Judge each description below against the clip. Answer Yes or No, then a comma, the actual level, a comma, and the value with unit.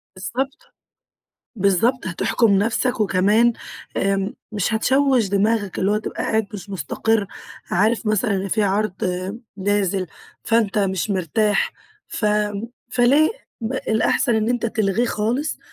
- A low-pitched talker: No, high, 215 Hz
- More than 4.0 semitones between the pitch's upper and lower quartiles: No, average, 2.9 semitones